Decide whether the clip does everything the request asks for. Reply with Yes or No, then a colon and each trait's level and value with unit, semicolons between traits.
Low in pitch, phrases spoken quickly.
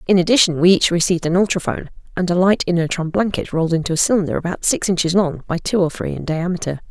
No: medium, 175 Hz; fast, 225 wpm